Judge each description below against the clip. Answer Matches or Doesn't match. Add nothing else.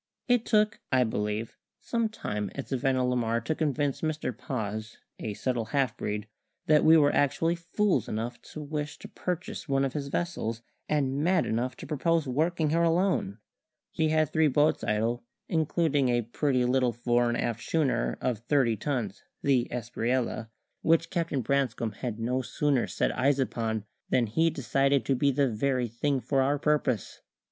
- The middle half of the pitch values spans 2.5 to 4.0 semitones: Doesn't match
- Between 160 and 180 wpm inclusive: Matches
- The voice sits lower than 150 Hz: Matches